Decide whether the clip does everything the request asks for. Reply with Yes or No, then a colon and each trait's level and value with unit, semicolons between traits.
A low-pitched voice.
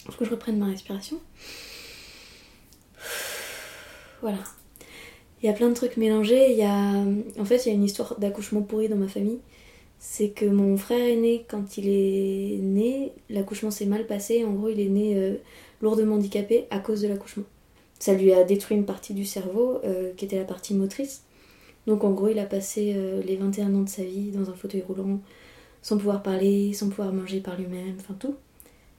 No: high, 205 Hz